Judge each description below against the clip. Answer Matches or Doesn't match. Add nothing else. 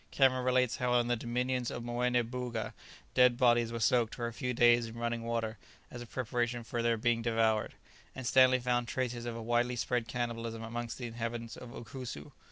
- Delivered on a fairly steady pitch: Matches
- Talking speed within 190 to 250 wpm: Matches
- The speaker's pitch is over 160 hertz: Doesn't match